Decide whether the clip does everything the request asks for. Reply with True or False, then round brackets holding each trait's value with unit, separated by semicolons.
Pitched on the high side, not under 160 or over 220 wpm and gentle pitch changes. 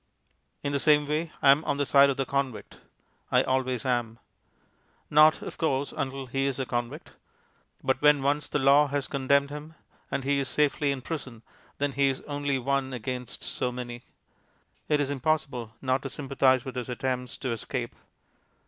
False (135 Hz; 180 wpm; 1.9 semitones)